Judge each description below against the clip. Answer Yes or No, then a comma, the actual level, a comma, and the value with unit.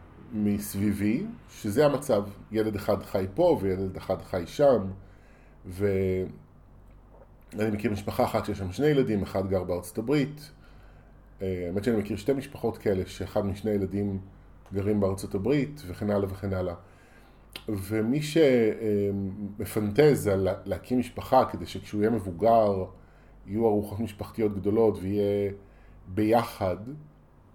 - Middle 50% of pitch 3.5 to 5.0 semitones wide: No, average, 2.8 semitones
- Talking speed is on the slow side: No, average, 120 wpm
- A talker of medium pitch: No, low, 100 Hz